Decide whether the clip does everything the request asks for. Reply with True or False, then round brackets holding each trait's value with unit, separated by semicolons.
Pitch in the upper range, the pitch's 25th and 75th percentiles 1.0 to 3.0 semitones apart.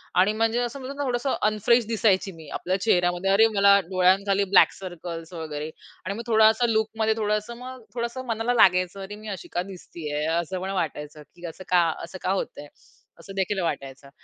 False (195 Hz; 4.0 semitones)